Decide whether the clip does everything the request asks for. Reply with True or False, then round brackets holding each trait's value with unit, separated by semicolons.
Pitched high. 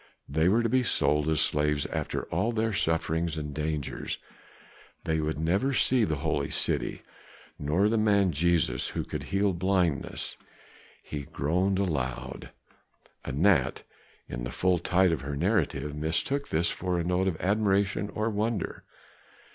False (85 Hz)